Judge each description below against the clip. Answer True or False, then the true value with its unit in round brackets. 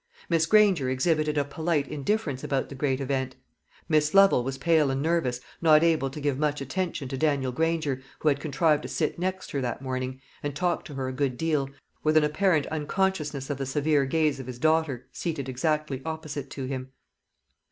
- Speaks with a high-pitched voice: False (145 Hz)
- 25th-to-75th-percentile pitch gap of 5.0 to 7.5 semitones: False (3.1 semitones)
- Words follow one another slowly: False (195 wpm)